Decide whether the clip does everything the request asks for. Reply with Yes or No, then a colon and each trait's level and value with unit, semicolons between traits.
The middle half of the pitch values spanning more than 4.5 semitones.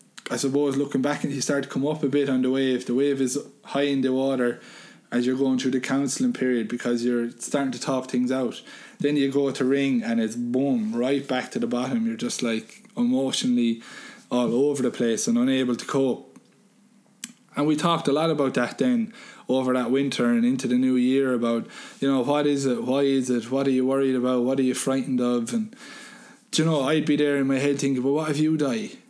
No: average, 2.7 semitones